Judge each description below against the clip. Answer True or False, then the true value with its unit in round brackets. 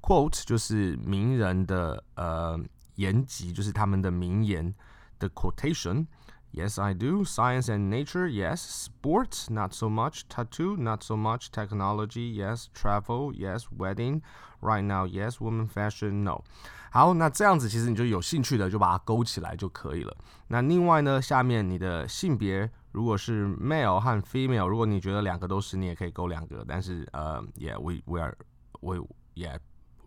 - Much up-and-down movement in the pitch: False (4.3 semitones)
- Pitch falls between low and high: False (105 Hz)